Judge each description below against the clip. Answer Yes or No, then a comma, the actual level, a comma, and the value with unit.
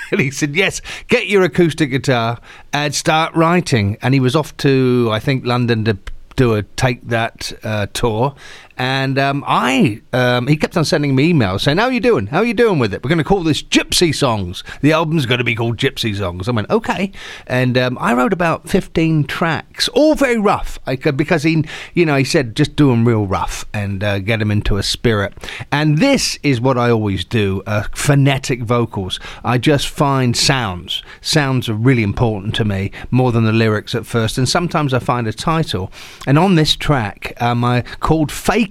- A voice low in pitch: Yes, low, 130 Hz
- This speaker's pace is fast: Yes, fast, 210 wpm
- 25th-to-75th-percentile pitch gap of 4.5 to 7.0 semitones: Yes, wide, 5.4 semitones